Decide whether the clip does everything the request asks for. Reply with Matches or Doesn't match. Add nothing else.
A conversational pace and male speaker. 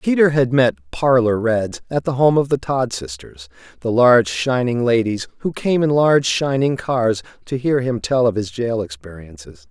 Matches